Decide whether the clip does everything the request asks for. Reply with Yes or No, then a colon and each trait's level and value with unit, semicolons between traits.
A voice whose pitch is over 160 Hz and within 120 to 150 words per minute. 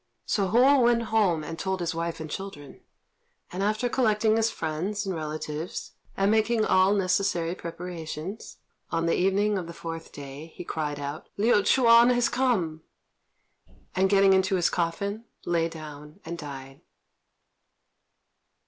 Yes: medium, 185 Hz; average, 145 wpm